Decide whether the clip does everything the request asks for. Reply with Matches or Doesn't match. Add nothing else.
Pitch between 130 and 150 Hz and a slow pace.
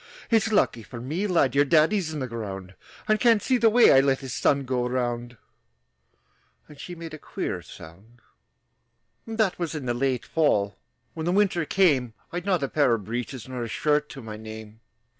Doesn't match